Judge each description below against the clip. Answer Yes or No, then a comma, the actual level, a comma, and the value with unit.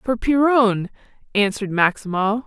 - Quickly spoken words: No, slow, 95 wpm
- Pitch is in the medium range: No, high, 220 Hz